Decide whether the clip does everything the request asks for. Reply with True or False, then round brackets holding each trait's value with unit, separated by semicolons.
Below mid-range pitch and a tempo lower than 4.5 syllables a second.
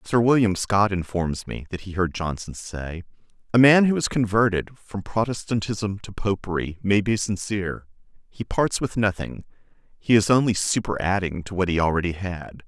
False (100 Hz; 4.9 syllables/s)